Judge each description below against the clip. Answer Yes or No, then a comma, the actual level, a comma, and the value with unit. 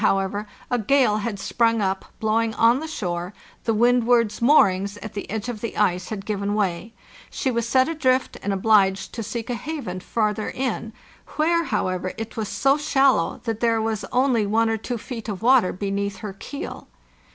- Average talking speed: Yes, average, 185 wpm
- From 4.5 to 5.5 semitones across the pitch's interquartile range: No, average, 3.4 semitones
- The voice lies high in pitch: Yes, high, 220 Hz